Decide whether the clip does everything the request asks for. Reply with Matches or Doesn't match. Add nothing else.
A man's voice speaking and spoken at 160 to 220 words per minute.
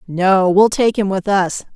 Doesn't match